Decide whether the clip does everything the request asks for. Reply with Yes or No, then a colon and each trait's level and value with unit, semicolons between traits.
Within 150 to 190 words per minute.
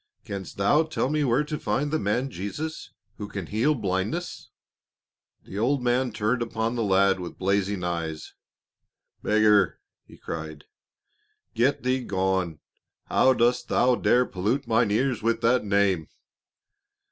No: average, 140 wpm